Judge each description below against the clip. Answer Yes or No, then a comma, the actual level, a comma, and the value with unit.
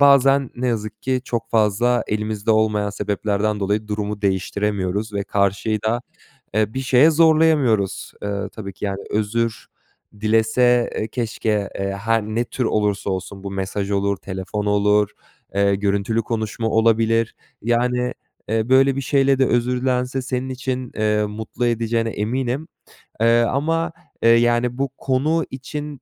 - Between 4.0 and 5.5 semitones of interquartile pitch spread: No, average, 3.4 semitones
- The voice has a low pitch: Yes, low, 110 Hz